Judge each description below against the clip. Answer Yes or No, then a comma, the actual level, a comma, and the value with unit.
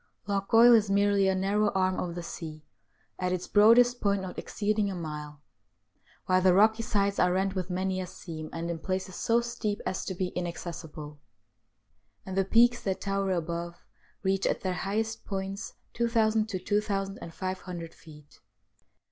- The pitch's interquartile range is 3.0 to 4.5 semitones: No, narrow, 2.6 semitones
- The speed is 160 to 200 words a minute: Yes, average, 165 wpm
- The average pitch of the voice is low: No, high, 190 Hz